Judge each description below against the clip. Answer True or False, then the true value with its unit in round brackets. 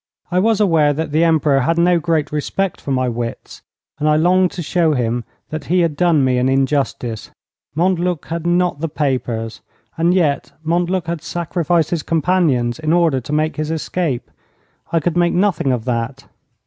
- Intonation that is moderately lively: True (4.2 semitones)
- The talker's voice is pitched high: False (160 Hz)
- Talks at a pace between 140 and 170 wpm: False (180 wpm)